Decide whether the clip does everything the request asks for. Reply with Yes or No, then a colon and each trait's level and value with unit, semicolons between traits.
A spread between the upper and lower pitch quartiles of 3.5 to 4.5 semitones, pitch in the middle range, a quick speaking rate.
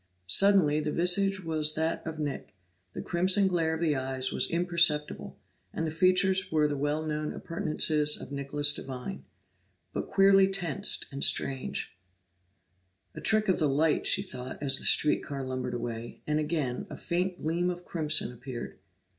No: average, 4.2 semitones; medium, 155 Hz; average, 165 wpm